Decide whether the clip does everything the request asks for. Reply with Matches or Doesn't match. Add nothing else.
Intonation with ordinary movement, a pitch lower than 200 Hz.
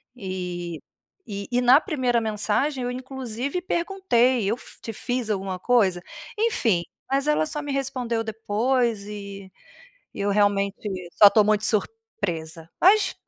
Doesn't match